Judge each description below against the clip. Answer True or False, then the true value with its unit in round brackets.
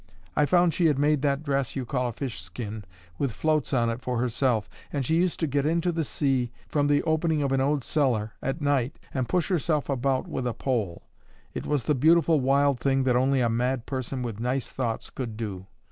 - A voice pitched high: False (135 Hz)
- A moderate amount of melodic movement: True (3.3 semitones)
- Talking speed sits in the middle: False (215 wpm)